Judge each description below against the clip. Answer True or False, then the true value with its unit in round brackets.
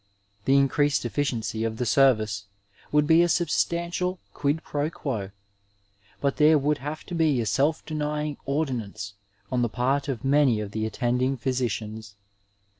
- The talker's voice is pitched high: False (135 Hz)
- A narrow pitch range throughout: False (4.8 semitones)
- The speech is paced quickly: False (155 wpm)